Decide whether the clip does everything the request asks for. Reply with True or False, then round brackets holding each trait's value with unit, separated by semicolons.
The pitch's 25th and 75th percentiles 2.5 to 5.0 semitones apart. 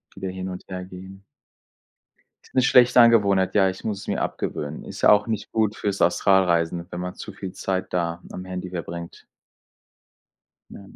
False (2.0 semitones)